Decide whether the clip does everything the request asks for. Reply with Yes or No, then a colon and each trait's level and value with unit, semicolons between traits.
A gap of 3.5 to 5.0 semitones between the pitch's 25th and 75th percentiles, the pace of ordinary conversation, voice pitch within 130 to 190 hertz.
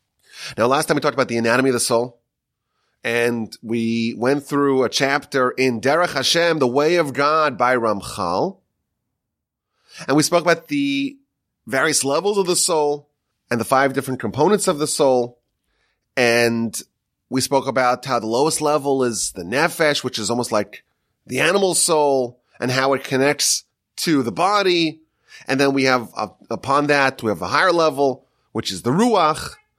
Yes: average, 4.1 semitones; average, 170 wpm; low, 135 Hz